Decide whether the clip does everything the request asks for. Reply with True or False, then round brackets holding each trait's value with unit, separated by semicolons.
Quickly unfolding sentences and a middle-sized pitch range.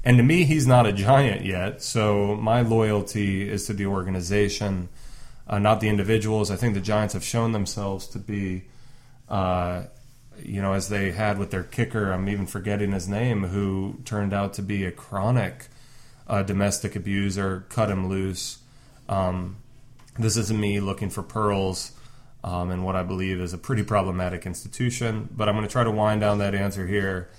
False (180 wpm; 3.1 semitones)